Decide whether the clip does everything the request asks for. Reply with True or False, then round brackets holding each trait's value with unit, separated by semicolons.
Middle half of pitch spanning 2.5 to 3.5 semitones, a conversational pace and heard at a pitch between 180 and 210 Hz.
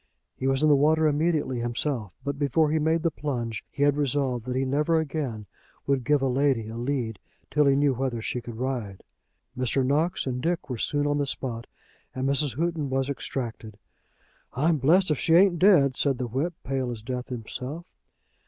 False (3.2 semitones; 195 wpm; 135 Hz)